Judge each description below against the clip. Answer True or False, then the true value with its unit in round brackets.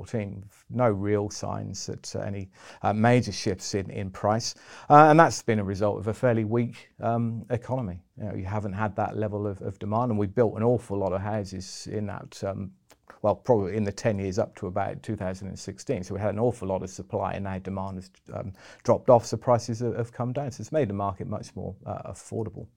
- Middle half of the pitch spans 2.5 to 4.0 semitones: True (3.0 semitones)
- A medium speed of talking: False (220 wpm)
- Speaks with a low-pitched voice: True (105 Hz)